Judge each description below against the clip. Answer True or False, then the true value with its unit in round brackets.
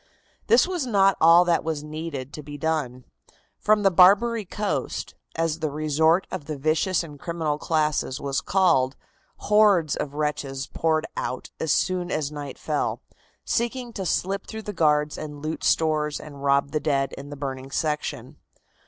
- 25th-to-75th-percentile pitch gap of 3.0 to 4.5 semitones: True (3.9 semitones)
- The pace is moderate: True (165 wpm)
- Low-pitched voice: False (155 Hz)